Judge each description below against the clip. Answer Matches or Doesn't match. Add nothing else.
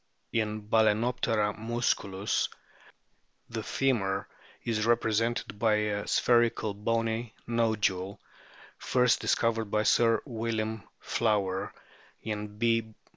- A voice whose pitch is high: Doesn't match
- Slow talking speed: Matches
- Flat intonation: Matches